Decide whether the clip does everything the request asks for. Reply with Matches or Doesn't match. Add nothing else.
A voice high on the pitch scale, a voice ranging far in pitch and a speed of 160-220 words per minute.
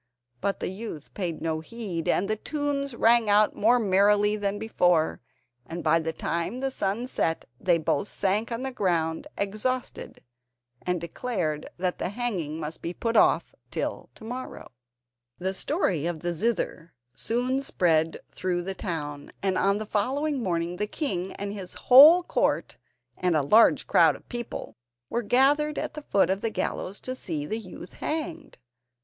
Matches